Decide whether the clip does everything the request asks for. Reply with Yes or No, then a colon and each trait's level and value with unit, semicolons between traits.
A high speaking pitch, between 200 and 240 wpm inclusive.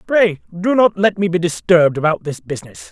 No: medium, 170 Hz; fast, 205 wpm